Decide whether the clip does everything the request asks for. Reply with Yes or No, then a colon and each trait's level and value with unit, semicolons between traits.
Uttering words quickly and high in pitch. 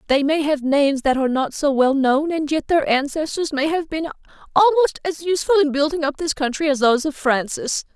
Yes: fast, 220 wpm; very high, 295 Hz